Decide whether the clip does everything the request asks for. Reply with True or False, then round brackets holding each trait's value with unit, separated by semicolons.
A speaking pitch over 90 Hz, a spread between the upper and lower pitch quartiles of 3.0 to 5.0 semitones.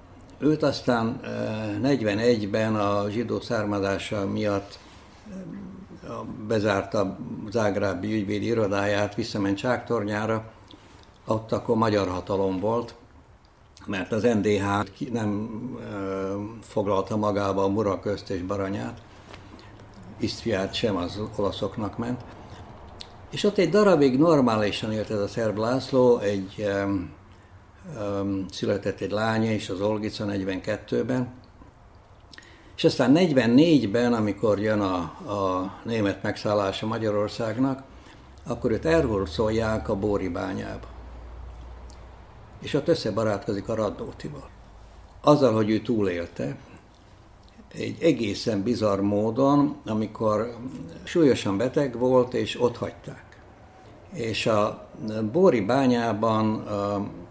False (105 Hz; 2.4 semitones)